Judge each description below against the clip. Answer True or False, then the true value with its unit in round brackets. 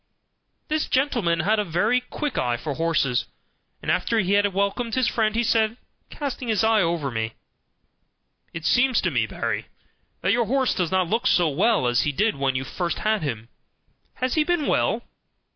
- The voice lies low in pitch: False (200 Hz)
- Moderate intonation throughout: False (6.9 semitones)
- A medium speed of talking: True (185 wpm)